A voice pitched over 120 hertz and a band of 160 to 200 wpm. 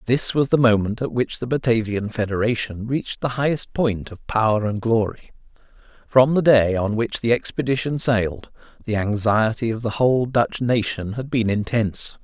No: low, 115 Hz; average, 170 wpm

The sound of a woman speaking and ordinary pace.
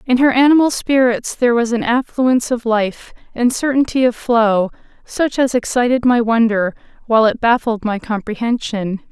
Yes: female; average, 160 wpm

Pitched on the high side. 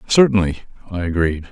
No: very low, 95 Hz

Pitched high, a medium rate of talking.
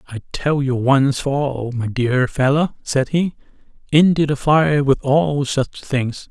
No: medium, 140 Hz; average, 170 wpm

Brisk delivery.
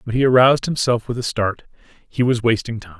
No: average, 180 wpm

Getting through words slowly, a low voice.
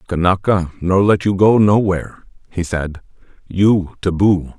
Yes: slow, 130 wpm; very low, 95 Hz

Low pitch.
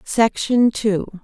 No: high, 215 Hz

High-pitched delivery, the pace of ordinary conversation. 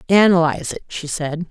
No: medium, 170 Hz; average, 160 wpm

